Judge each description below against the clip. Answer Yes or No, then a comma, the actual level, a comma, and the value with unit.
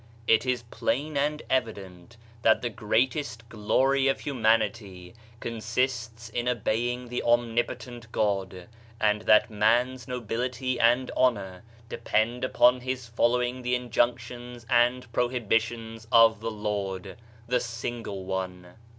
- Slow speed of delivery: Yes, slow, 115 wpm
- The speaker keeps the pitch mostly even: Yes, narrow, 2.2 semitones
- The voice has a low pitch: Yes, low, 120 Hz